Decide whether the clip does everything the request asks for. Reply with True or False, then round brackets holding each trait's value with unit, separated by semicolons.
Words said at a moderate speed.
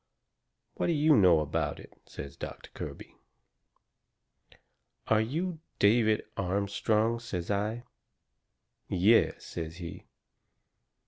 False (100 wpm)